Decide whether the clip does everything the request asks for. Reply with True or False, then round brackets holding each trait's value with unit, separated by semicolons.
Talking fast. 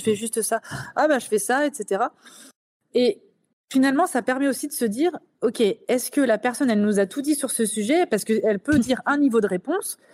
True (230 wpm)